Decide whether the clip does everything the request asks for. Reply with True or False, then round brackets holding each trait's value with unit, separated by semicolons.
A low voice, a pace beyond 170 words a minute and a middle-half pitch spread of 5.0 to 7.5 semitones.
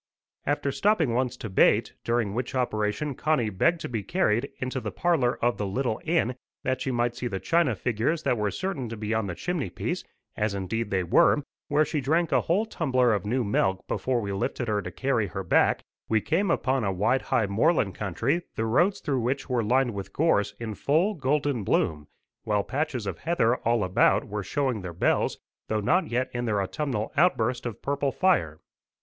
True (120 Hz; 200 wpm; 5.4 semitones)